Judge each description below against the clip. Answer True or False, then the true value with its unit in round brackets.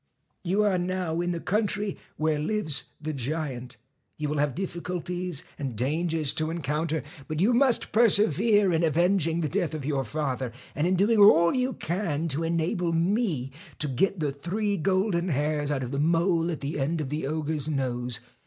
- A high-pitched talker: False (165 Hz)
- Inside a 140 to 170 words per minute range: False (180 wpm)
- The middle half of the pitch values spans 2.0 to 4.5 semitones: True (4.0 semitones)